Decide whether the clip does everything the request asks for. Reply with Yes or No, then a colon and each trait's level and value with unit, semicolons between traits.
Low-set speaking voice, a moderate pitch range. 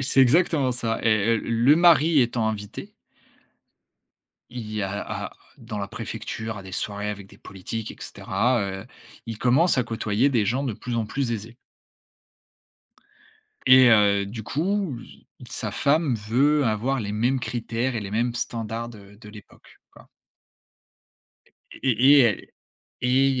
Yes: low, 115 Hz; average, 3.7 semitones